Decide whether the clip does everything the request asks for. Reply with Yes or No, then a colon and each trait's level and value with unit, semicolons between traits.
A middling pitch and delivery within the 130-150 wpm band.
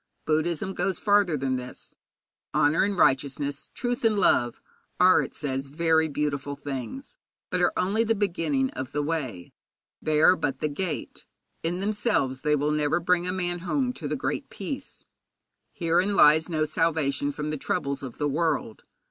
No: medium, 155 Hz; average, 165 wpm